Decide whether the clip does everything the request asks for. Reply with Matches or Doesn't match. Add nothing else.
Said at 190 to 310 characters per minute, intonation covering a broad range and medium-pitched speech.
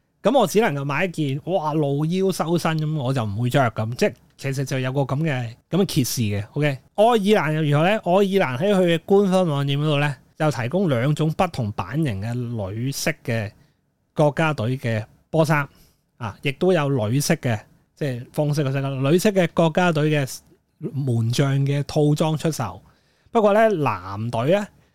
Doesn't match